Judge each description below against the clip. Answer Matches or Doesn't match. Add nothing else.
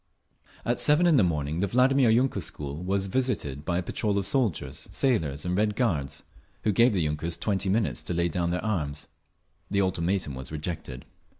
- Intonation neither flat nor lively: Doesn't match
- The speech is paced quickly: Doesn't match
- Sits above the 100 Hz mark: Doesn't match